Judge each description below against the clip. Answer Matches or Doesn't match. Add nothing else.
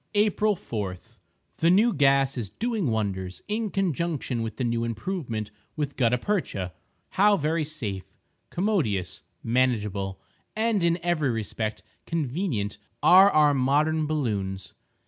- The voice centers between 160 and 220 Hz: Doesn't match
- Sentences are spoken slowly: Matches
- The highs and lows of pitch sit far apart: Matches